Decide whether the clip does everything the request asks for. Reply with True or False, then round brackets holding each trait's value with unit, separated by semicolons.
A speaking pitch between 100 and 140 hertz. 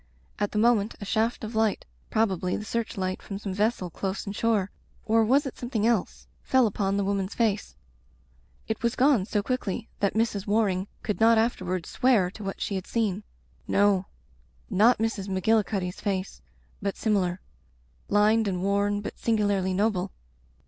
False (205 Hz)